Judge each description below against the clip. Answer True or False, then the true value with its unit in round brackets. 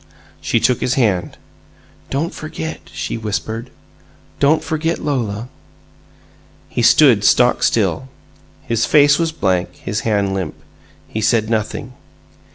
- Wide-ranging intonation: True (5.7 semitones)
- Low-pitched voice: True (115 Hz)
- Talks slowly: True (120 wpm)